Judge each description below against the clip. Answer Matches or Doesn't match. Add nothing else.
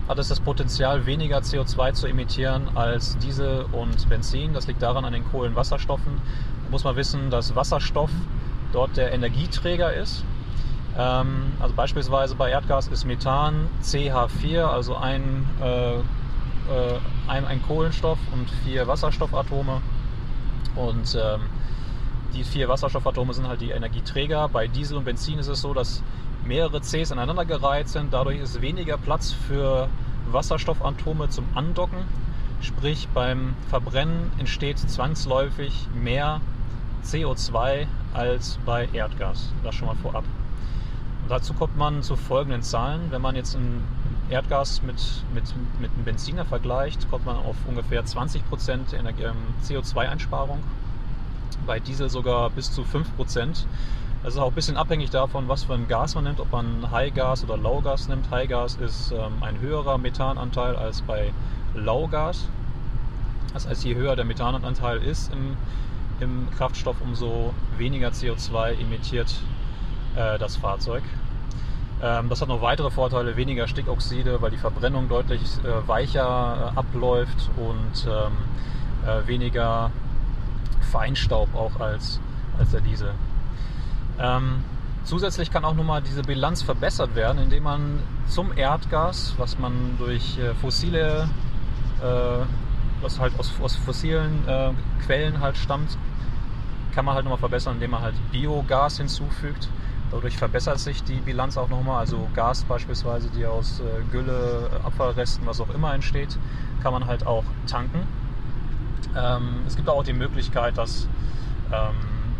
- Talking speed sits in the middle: Matches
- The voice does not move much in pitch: Matches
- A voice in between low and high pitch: Doesn't match